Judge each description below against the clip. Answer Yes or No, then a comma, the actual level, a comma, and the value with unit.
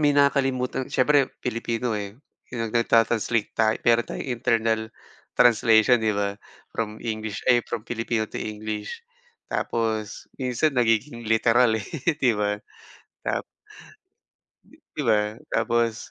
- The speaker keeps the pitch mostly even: Yes, narrow, 2.0 semitones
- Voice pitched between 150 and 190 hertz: No, low, 115 Hz